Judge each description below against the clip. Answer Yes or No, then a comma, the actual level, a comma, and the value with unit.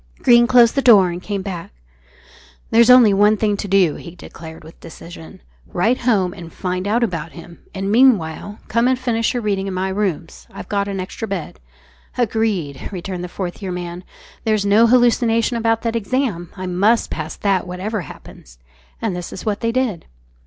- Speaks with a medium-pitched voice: No, high, 200 Hz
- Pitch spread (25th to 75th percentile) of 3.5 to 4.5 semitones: Yes, average, 4.2 semitones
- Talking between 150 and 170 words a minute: No, average, 185 wpm